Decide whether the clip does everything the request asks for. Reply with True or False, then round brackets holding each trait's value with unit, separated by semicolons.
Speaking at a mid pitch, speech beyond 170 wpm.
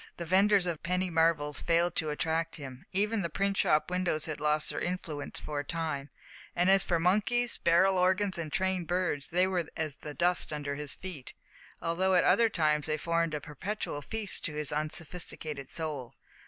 True (165 Hz; 185 wpm)